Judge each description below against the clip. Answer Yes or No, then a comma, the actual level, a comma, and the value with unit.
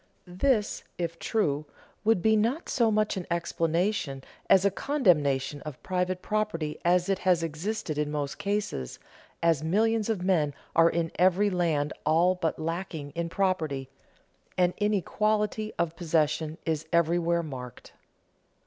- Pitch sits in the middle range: Yes, medium, 170 Hz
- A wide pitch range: No, average, 4.4 semitones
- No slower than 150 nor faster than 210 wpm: No, average, 140 wpm